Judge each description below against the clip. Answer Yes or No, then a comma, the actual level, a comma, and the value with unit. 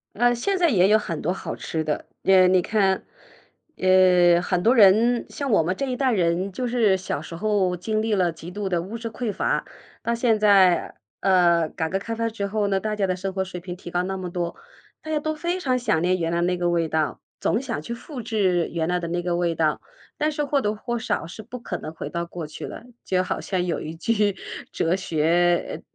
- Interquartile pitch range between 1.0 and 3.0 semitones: No, average, 4.3 semitones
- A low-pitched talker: No, high, 190 Hz